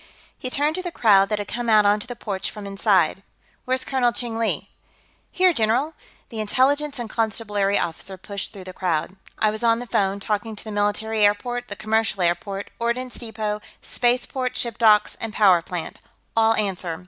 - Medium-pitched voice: No, high, 215 Hz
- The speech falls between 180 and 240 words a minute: Yes, average, 185 wpm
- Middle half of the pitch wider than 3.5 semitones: No, average, 3.1 semitones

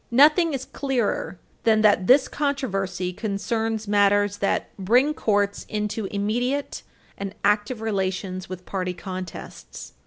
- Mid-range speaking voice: No, high, 205 Hz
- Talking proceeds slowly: Yes, slow, 120 wpm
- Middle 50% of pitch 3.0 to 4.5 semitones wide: Yes, average, 3.8 semitones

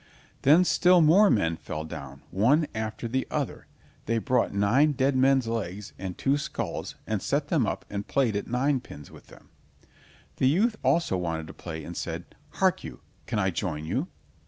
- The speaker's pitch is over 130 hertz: No, low, 115 Hz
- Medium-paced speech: Yes, average, 180 wpm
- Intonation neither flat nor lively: No, wide, 7.7 semitones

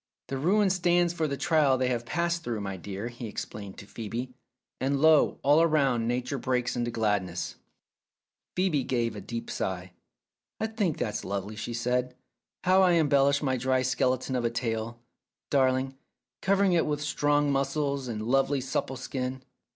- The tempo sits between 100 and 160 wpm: No, average, 170 wpm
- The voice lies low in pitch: Yes, low, 130 Hz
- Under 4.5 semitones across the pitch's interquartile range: Yes, average, 4.0 semitones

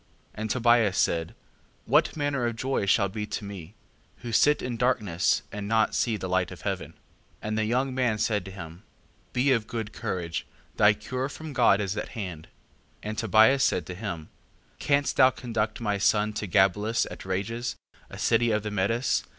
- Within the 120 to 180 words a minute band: No, average, 190 wpm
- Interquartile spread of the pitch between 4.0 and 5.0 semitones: No, average, 3.3 semitones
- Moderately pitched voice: No, low, 110 Hz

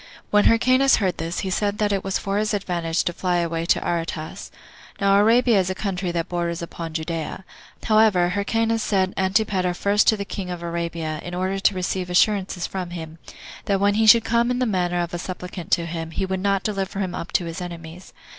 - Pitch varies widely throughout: No, average, 2.9 semitones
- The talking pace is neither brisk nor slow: No, fast, 210 wpm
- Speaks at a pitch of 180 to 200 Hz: Yes, medium, 185 Hz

